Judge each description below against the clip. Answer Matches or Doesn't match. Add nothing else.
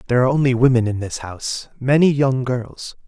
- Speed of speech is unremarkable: Matches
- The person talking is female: Doesn't match